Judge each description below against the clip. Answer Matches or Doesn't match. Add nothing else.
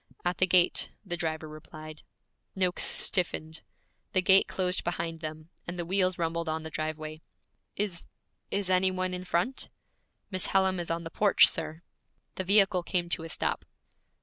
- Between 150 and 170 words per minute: Matches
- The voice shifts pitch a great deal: Doesn't match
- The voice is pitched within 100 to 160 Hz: Doesn't match